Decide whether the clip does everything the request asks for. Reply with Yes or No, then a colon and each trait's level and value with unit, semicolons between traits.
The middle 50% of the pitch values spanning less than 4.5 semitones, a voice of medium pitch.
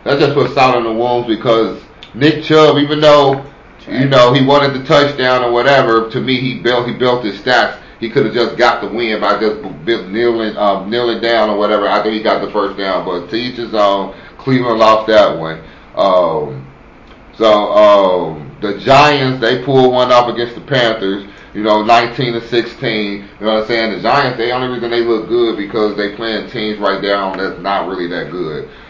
No: average, 3.5 semitones; low, 115 Hz